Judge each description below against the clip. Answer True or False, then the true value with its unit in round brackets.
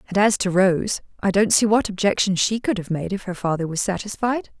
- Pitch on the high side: True (195 Hz)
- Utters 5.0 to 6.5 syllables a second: True (5.5 syllables/s)